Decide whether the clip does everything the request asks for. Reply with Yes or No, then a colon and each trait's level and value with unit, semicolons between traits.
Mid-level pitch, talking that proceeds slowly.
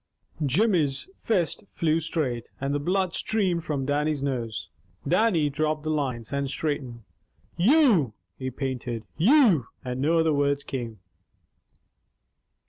Yes: medium, 145 Hz; slow, 130 wpm